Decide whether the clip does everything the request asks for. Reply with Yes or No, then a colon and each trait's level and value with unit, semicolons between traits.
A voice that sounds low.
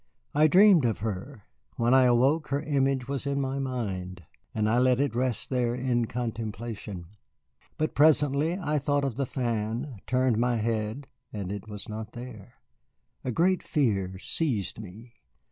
Yes: low, 125 Hz